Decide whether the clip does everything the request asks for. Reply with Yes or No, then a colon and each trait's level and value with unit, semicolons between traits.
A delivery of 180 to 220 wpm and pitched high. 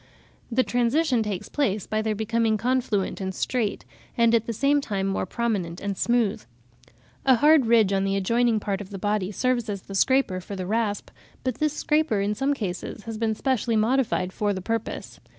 Yes: average, 190 wpm; high, 220 Hz